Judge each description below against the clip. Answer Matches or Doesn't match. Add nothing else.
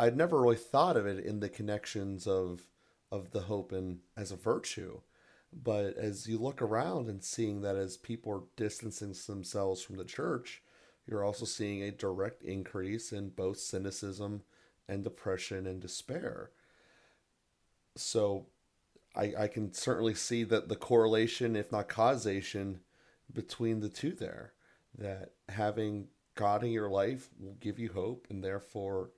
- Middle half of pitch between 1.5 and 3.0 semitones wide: Matches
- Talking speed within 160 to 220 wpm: Doesn't match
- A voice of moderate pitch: Doesn't match